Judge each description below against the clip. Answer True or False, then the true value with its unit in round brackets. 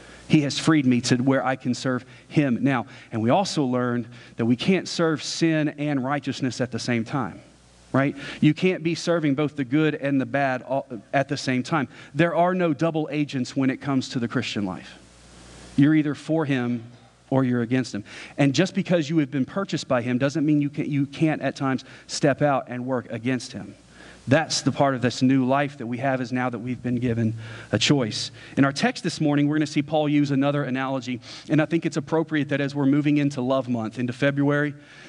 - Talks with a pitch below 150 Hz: True (135 Hz)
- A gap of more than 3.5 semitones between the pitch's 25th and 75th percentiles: False (3.2 semitones)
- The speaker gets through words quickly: True (220 wpm)